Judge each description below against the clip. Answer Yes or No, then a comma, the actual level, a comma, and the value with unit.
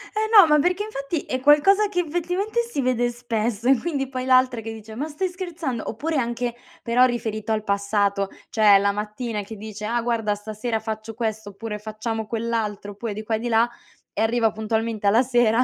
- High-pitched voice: Yes, high, 230 Hz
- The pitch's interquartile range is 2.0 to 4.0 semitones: Yes, average, 3.5 semitones